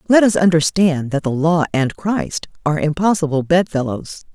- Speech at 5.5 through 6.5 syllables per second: No, 5.0 syllables/s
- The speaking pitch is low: No, medium, 165 Hz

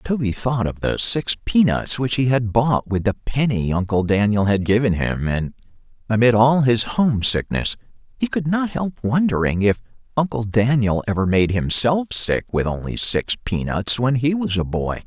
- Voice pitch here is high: No, low, 115 Hz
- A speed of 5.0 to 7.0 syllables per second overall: No, 4.6 syllables/s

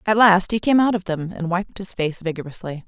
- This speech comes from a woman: Yes, female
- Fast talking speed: Yes, fast, 250 wpm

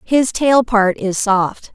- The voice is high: Yes, high, 220 Hz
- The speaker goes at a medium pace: Yes, average, 170 wpm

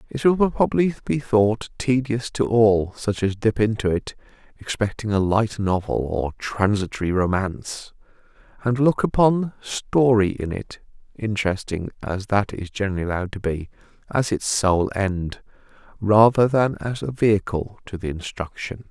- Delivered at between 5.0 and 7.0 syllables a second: No, 3.8 syllables/s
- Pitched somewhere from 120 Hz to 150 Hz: No, low, 105 Hz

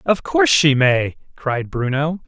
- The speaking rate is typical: Yes, average, 160 wpm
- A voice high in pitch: No, low, 130 Hz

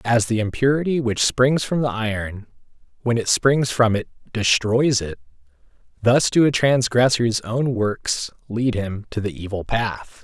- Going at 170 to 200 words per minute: No, average, 160 wpm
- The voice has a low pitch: Yes, low, 115 Hz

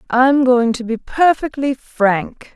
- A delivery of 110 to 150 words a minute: Yes, average, 140 wpm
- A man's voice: No, female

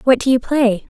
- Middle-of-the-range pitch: No, very high, 250 Hz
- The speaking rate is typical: No, fast, 240 wpm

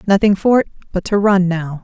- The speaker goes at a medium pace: No, fast, 230 wpm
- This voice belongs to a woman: Yes, female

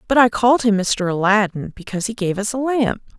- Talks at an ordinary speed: No, fast, 225 wpm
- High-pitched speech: Yes, high, 215 Hz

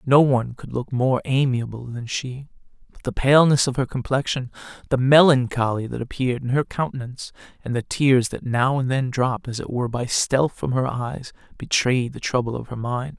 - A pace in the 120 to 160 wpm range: No, average, 195 wpm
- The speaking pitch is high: No, low, 130 Hz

